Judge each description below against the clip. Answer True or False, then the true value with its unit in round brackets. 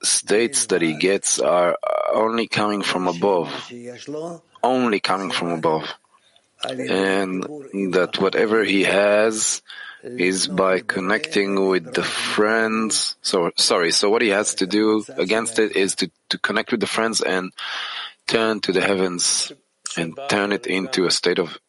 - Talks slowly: False (145 wpm)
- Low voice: True (100 Hz)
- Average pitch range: True (3.0 semitones)